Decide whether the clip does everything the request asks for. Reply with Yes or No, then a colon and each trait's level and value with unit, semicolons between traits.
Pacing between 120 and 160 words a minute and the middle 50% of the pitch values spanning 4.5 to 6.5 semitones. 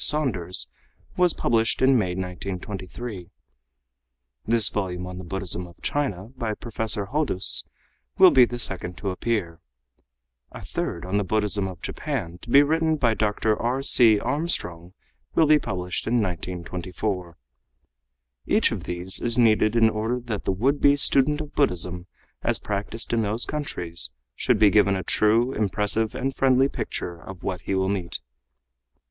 Yes: average, 155 wpm; average, 5.0 semitones